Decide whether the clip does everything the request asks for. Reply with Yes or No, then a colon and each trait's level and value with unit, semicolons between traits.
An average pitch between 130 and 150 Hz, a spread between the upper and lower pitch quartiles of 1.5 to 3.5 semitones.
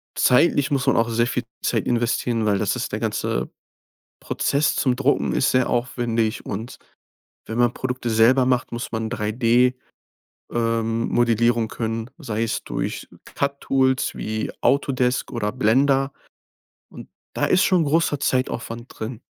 No: low, 120 Hz; narrow, 2.4 semitones